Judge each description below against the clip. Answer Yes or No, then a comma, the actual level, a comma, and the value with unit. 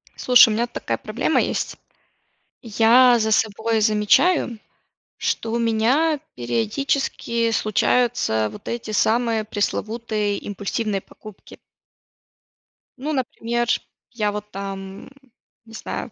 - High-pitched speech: Yes, high, 225 Hz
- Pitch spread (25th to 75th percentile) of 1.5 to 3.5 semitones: Yes, narrow, 2.4 semitones